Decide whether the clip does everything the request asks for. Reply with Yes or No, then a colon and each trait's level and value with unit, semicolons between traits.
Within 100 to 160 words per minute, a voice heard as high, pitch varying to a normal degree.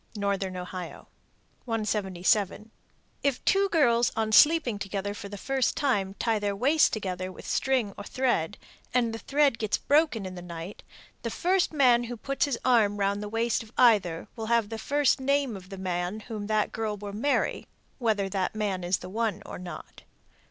No: average, 180 wpm; high, 215 Hz; average, 3.9 semitones